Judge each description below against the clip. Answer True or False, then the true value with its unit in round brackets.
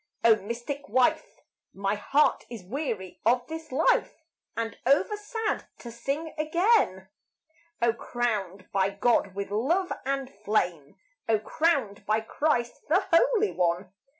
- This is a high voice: True (235 Hz)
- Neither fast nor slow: False (130 wpm)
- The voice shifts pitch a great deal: True (7.4 semitones)